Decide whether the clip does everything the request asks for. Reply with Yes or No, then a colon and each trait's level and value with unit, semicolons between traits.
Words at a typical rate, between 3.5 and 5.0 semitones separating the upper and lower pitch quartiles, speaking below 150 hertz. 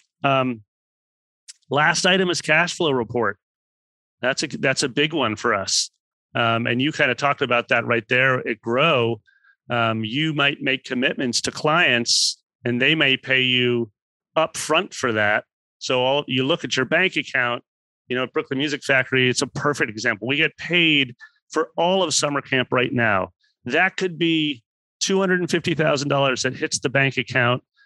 Yes: average, 170 wpm; average, 4.4 semitones; low, 135 Hz